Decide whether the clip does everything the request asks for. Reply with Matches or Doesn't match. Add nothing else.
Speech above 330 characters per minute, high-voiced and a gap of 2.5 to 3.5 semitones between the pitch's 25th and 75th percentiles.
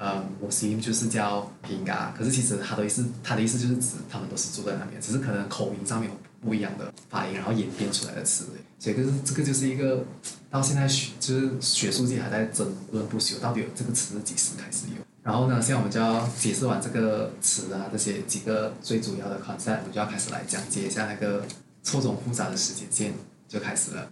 Doesn't match